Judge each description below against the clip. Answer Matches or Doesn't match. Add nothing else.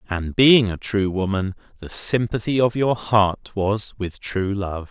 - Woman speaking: Doesn't match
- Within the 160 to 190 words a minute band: Matches